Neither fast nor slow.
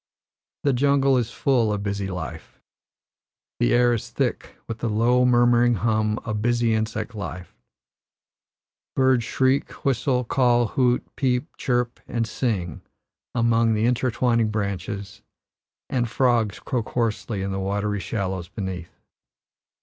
No: slow, 125 wpm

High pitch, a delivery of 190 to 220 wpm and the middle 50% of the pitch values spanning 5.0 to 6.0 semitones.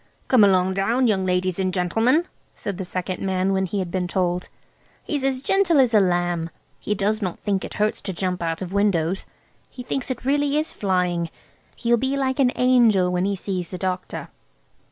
Yes: high, 195 Hz; average, 195 wpm; average, 5.3 semitones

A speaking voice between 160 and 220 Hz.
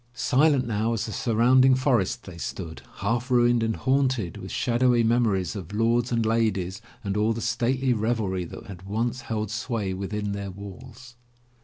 No: low, 115 Hz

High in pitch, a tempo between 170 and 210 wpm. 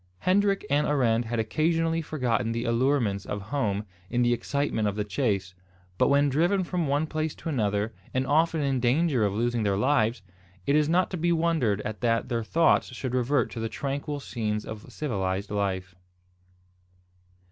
No: low, 125 Hz; average, 175 wpm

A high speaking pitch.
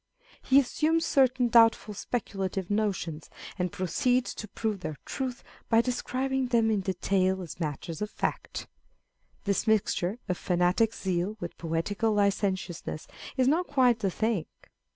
Yes: high, 210 Hz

